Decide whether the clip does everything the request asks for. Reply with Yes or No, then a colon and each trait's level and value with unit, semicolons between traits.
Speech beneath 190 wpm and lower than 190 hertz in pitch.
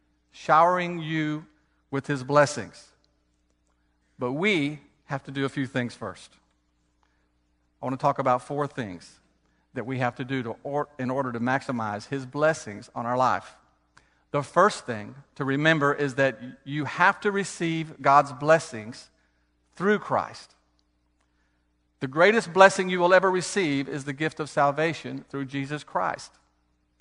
Yes: average, 150 wpm; low, 135 Hz